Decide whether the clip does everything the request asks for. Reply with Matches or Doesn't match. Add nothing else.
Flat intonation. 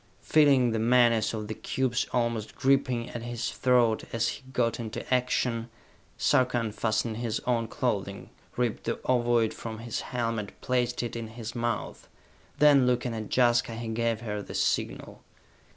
Matches